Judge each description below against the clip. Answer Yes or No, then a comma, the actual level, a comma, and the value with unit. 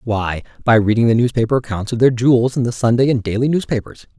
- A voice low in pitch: Yes, low, 120 Hz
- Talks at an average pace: No, fast, 215 wpm